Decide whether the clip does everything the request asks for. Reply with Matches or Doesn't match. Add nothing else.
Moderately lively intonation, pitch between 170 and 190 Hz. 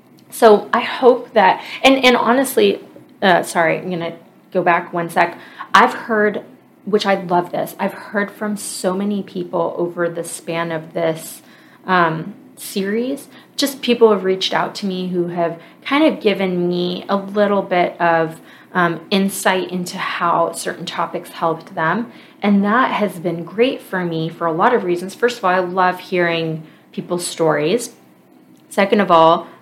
Matches